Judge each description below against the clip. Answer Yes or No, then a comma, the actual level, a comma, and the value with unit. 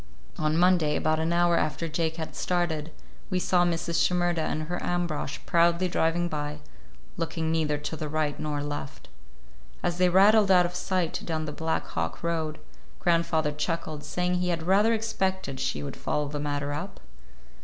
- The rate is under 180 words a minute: Yes, average, 170 wpm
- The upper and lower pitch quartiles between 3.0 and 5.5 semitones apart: No, narrow, 2.5 semitones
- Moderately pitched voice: Yes, medium, 165 Hz